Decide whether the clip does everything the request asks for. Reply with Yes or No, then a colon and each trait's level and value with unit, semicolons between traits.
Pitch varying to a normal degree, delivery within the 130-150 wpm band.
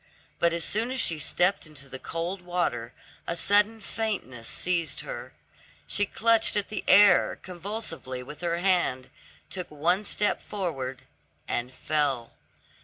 No: wide, 6.1 semitones; average, 140 wpm